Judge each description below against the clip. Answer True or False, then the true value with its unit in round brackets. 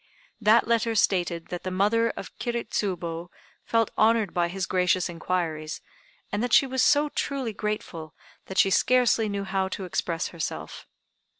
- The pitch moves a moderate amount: True (4.6 semitones)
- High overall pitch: True (195 Hz)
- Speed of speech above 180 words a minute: False (160 wpm)